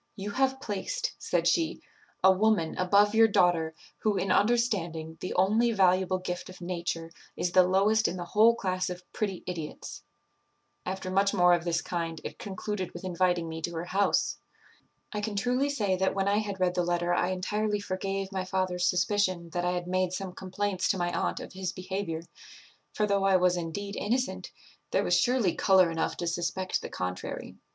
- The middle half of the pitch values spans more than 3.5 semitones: No, narrow, 2.5 semitones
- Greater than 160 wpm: Yes, average, 190 wpm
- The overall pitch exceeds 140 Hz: Yes, medium, 185 Hz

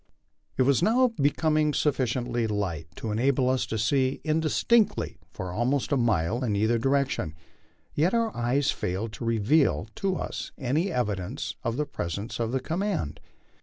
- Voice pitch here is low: Yes, low, 130 Hz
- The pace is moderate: Yes, average, 160 wpm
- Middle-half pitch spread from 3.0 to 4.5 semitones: No, wide, 5.5 semitones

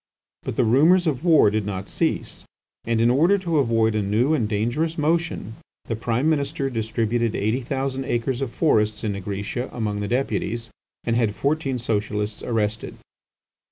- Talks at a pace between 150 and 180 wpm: Yes, average, 160 wpm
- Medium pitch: No, low, 120 Hz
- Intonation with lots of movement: No, average, 4.3 semitones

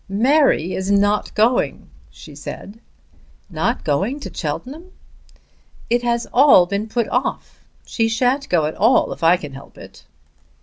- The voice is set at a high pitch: Yes, high, 225 Hz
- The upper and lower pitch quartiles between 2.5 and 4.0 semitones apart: No, average, 5.2 semitones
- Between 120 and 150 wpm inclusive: Yes, average, 145 wpm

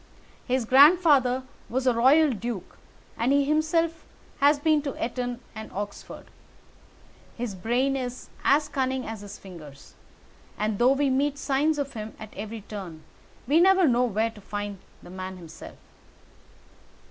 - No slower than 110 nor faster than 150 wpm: Yes, average, 145 wpm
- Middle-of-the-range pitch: No, very high, 250 Hz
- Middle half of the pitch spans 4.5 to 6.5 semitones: Yes, average, 5.1 semitones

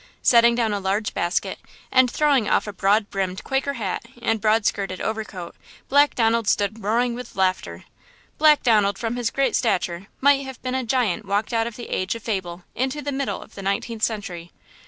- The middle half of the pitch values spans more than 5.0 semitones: No, average, 4.1 semitones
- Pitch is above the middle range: Yes, high, 225 Hz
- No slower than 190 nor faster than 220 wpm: Yes, average, 195 wpm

